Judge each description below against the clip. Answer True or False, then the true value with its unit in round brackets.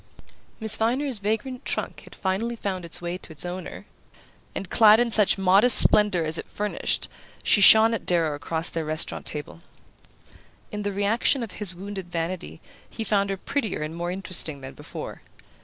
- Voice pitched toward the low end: False (195 Hz)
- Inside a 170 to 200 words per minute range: True (175 wpm)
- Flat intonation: False (4.3 semitones)